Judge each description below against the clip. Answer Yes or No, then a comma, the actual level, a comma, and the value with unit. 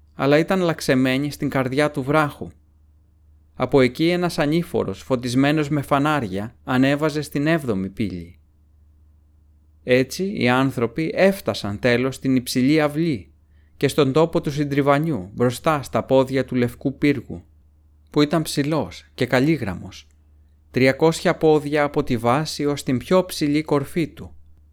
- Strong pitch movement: Yes, wide, 8.2 semitones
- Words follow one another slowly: No, average, 130 wpm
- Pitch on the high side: No, low, 130 Hz